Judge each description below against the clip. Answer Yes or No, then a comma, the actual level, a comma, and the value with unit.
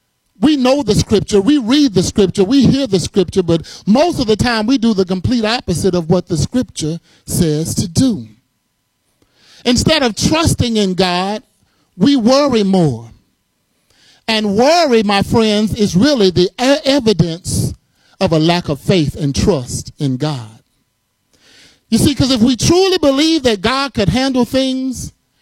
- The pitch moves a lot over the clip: Yes, wide, 6.6 semitones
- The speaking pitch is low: No, high, 210 Hz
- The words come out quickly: No, average, 155 wpm